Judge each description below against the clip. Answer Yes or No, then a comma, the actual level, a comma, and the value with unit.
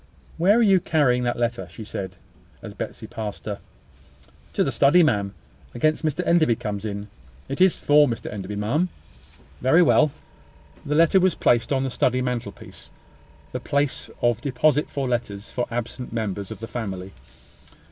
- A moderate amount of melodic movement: No, wide, 5.9 semitones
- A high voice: No, low, 125 Hz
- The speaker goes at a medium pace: Yes, average, 165 wpm